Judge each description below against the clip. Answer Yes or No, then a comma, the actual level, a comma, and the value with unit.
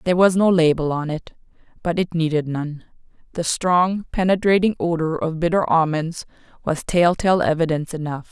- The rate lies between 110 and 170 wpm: Yes, average, 145 wpm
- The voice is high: No, medium, 165 Hz